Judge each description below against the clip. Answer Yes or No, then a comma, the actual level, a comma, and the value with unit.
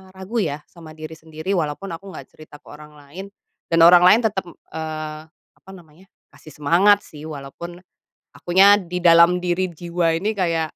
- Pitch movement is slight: No, average, 3.0 semitones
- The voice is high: No, medium, 170 Hz